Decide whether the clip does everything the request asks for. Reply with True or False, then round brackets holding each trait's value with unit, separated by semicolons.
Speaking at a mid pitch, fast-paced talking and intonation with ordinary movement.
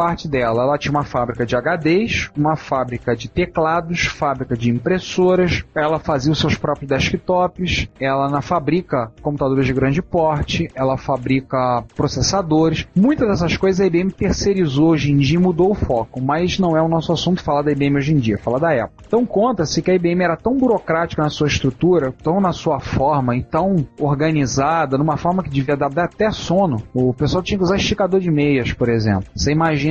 True (155 Hz; 195 wpm; 4.7 semitones)